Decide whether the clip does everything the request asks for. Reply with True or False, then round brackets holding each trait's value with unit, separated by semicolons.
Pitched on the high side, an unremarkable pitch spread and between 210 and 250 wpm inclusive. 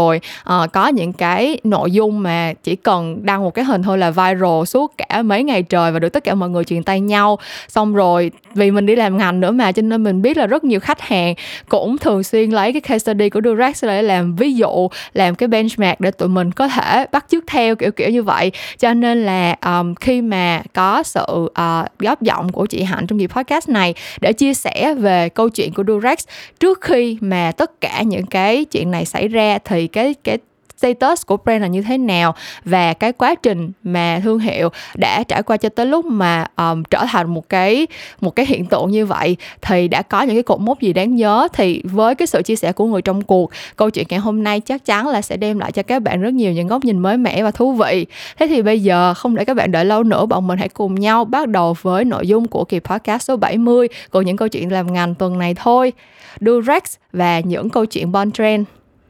True (205 Hz; 4.6 semitones; 240 wpm)